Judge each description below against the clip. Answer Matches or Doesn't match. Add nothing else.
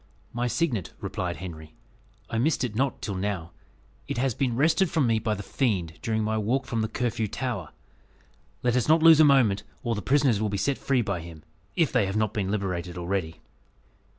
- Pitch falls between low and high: Doesn't match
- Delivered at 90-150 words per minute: Doesn't match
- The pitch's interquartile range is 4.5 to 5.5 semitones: Matches